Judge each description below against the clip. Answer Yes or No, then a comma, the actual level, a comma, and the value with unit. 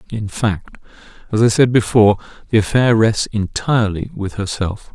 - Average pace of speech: Yes, average, 145 wpm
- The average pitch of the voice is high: No, low, 110 Hz